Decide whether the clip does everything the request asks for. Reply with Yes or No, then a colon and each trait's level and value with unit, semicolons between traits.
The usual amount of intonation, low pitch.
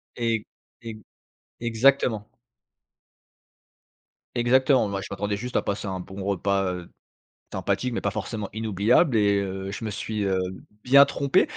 Yes: average, 3.2 semitones; low, 105 Hz